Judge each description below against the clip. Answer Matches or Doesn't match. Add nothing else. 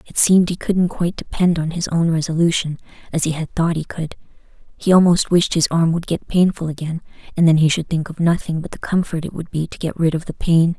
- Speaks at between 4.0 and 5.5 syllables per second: Doesn't match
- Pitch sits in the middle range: Matches